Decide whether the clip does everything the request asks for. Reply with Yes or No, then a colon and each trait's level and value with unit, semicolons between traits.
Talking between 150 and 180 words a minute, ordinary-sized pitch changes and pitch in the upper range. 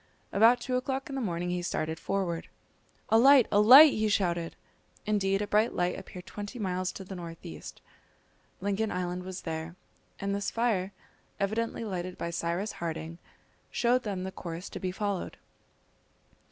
Yes: average, 165 wpm; average, 3.6 semitones; high, 195 Hz